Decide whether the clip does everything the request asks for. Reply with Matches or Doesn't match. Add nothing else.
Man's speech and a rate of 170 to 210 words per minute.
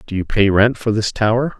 Doesn't match